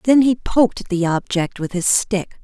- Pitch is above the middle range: Yes, high, 205 Hz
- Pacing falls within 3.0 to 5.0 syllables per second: Yes, 4.3 syllables/s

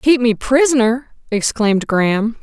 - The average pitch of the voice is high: Yes, high, 240 Hz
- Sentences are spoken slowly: Yes, slow, 125 wpm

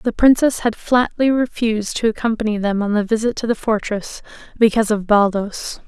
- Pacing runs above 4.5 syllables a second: Yes, 5.3 syllables/s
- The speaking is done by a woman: Yes, female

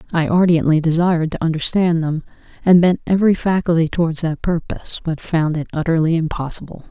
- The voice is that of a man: No, female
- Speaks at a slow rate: No, average, 155 wpm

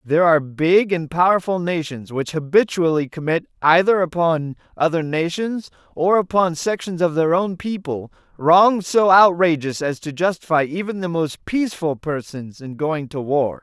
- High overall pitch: No, medium, 165 Hz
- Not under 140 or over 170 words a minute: Yes, average, 155 wpm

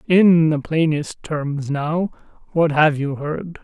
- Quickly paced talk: No, average, 150 wpm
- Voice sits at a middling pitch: Yes, medium, 155 Hz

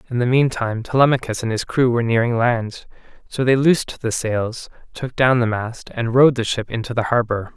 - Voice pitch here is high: No, low, 120 Hz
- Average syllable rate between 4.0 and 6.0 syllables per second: Yes, 5.3 syllables/s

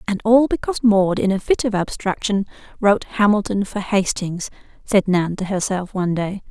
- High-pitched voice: Yes, high, 200 Hz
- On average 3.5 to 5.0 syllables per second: No, 5.4 syllables/s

